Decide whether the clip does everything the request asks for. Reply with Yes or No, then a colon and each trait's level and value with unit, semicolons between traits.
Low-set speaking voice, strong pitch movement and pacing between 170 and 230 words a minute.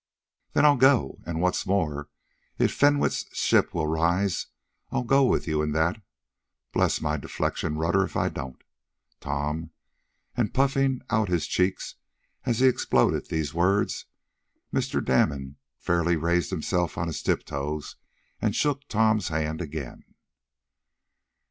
No: very low, 85 Hz; wide, 6.0 semitones; slow, 135 wpm